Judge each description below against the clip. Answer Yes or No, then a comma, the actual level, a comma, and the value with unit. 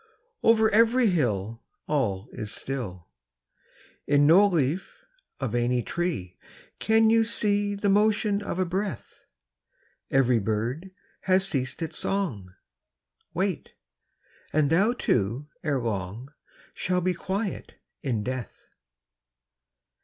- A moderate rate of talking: No, slow, 115 wpm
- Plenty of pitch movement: Yes, wide, 8.8 semitones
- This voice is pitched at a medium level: Yes, medium, 155 Hz